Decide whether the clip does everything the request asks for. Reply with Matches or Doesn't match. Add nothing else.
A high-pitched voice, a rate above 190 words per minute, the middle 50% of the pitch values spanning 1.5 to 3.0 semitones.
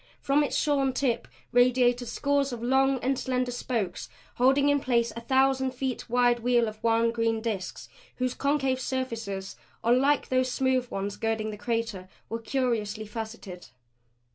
Doesn't match